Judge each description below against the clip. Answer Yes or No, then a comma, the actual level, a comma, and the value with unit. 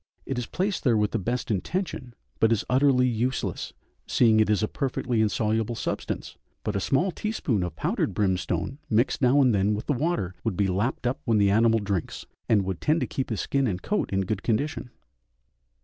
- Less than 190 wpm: No, average, 200 wpm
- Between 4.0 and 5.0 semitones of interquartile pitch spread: Yes, average, 4.3 semitones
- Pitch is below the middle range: Yes, low, 115 Hz